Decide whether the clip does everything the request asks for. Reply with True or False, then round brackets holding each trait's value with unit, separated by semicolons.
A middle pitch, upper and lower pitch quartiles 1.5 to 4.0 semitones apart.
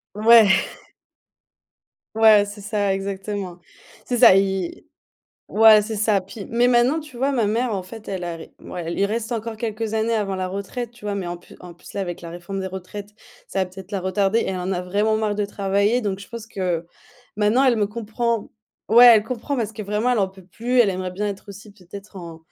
False (205 Hz; 2.8 semitones)